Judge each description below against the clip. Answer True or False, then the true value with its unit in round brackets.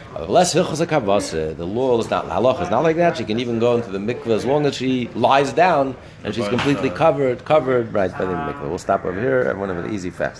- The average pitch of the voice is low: True (125 Hz)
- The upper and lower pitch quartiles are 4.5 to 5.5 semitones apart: True (4.9 semitones)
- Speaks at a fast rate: True (225 wpm)